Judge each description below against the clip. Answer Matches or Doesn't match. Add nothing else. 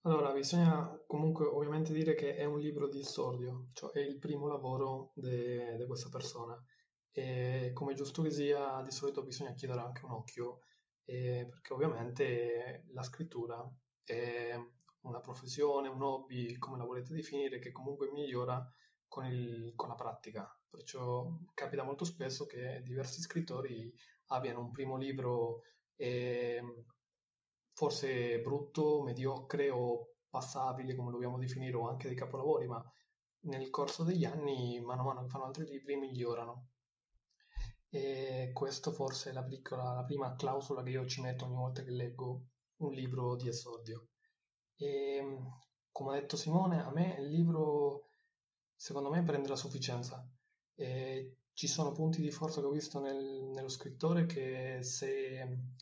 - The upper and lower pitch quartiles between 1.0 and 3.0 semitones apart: Matches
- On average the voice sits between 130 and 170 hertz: Matches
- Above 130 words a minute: Matches